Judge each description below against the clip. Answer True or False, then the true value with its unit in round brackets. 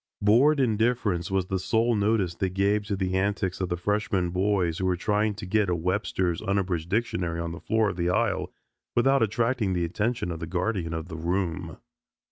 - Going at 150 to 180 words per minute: False (195 wpm)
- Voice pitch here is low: True (95 Hz)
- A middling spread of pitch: True (3.5 semitones)